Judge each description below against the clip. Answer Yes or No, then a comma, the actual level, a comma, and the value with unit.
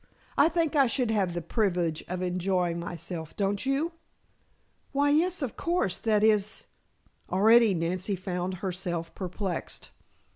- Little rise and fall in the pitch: No, average, 4.7 semitones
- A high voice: Yes, high, 195 Hz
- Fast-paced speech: No, average, 140 wpm